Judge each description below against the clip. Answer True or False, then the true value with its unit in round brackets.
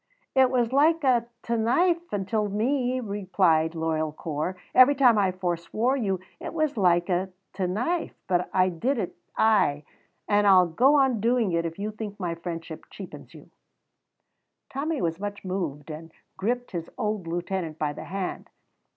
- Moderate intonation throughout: False (6.1 semitones)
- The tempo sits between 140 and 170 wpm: True (165 wpm)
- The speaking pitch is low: False (200 Hz)